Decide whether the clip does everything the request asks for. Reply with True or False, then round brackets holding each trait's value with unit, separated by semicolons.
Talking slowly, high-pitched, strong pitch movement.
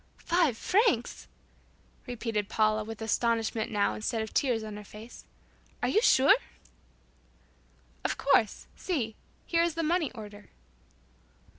True (125 wpm; 230 Hz; 5.8 semitones)